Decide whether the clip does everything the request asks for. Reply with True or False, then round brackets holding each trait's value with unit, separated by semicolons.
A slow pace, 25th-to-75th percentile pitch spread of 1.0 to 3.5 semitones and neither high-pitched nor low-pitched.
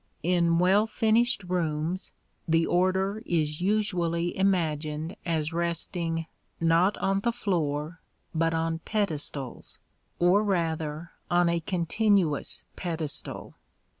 True (105 wpm; 2.8 semitones; 170 Hz)